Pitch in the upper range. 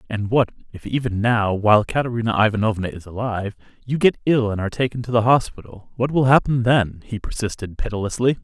No: low, 115 Hz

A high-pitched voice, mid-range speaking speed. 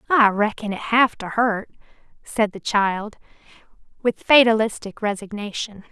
No: high, 215 Hz; slow, 120 wpm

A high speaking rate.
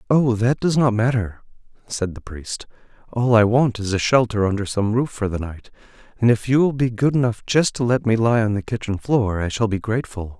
Yes: fast, 230 wpm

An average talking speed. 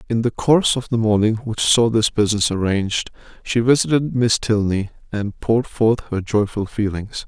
Yes: average, 175 wpm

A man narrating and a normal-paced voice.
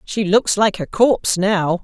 No: female; average, 195 wpm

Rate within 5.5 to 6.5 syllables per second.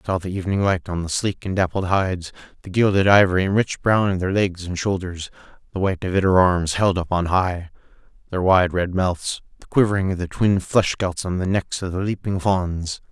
Yes: 5.6 syllables/s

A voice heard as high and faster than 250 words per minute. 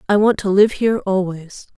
No: high, 195 Hz; average, 200 wpm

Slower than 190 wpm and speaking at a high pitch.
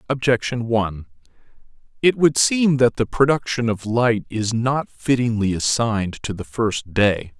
No: average, 145 wpm; low, 120 Hz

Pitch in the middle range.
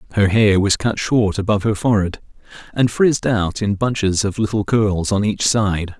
No: low, 105 Hz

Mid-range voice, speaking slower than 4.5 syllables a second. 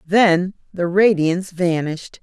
Yes: medium, 180 Hz; 4.1 syllables/s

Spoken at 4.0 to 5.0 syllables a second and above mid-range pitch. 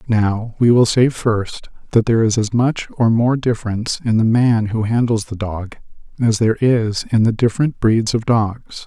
No: 4.7 syllables/s; low, 115 Hz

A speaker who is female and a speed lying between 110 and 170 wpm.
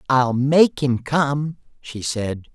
No: male; average, 140 wpm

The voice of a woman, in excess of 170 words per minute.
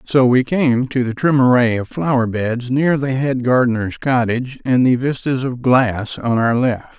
No: male; average, 195 wpm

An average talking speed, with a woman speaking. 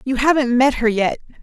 No: fast, 210 wpm; female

